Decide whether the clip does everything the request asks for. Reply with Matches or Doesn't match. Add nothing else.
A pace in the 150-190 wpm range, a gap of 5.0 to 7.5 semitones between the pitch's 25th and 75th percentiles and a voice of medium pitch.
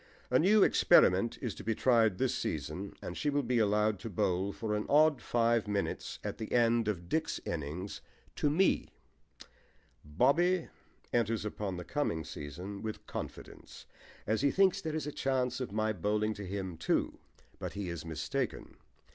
Doesn't match